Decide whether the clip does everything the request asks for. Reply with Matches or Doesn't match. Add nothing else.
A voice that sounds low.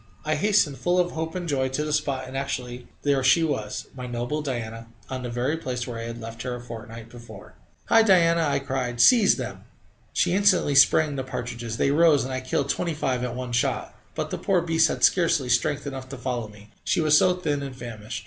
Matches